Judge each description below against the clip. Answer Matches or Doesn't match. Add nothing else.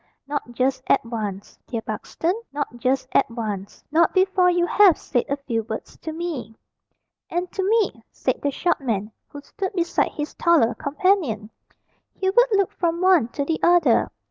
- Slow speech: Doesn't match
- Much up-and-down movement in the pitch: Matches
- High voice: Matches